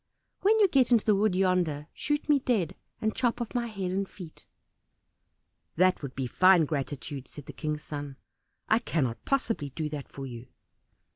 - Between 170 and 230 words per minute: Yes, average, 180 wpm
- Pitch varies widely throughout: Yes, wide, 7.8 semitones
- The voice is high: No, medium, 180 Hz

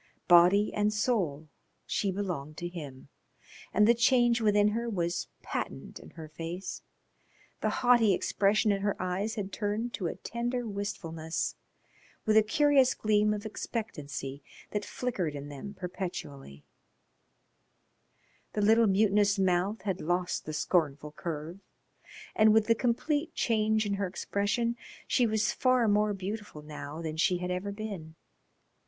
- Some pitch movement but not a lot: Yes, average, 4.0 semitones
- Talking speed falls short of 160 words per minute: Yes, average, 140 wpm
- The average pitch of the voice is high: Yes, high, 200 Hz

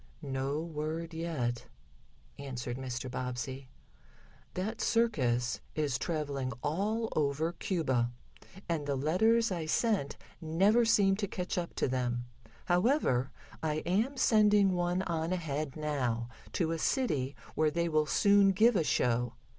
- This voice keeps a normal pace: No, slow, 130 wpm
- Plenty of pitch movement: Yes, wide, 6.2 semitones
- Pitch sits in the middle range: Yes, medium, 160 Hz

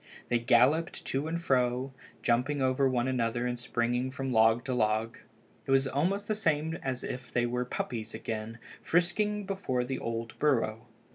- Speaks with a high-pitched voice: No, low, 125 Hz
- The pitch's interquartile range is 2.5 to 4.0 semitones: Yes, average, 3.6 semitones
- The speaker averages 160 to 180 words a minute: Yes, average, 165 wpm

